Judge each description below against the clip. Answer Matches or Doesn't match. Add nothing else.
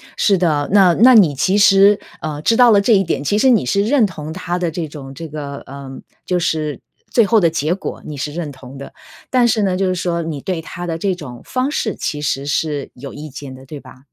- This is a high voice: Doesn't match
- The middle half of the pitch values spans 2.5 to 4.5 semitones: Doesn't match